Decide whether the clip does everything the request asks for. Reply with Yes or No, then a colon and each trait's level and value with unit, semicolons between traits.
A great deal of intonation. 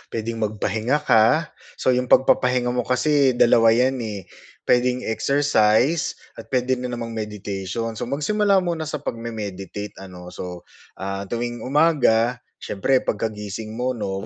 No: average, 3.4 semitones